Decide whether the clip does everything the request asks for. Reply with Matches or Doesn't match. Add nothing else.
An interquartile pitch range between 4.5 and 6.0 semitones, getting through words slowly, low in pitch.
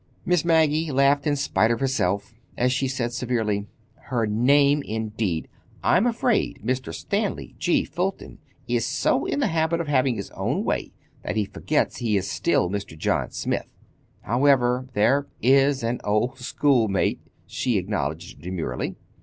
Doesn't match